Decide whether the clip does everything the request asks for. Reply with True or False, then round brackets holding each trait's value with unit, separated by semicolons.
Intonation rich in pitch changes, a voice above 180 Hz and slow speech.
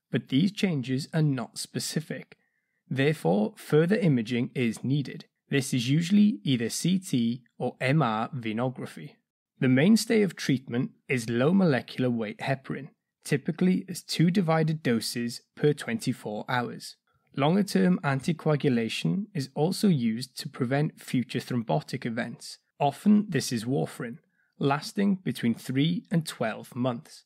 False (6.2 semitones; 145 Hz; 125 wpm)